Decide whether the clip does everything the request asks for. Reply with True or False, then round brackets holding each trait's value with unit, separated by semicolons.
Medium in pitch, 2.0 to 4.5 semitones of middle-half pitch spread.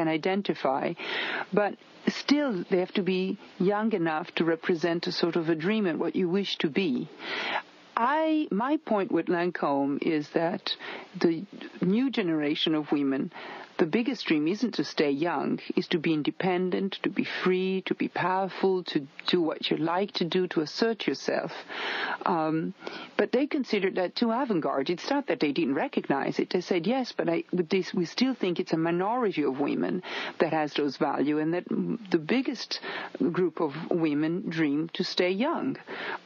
True (180 Hz; 4.0 semitones)